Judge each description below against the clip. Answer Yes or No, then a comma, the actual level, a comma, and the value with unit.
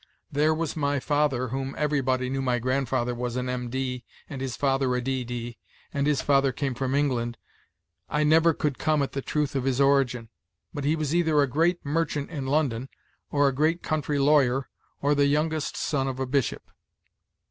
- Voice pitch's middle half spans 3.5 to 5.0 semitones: No, narrow, 2.6 semitones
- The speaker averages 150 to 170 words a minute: No, average, 190 wpm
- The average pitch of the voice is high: No, medium, 140 Hz